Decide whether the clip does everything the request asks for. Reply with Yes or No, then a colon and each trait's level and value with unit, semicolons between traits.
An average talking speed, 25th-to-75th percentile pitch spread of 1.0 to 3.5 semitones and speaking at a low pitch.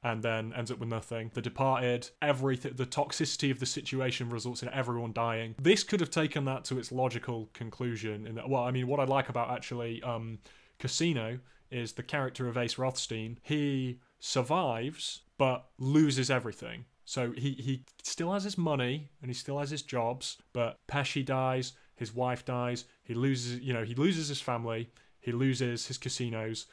Yes: average, 180 wpm; average, 2.7 semitones; low, 130 Hz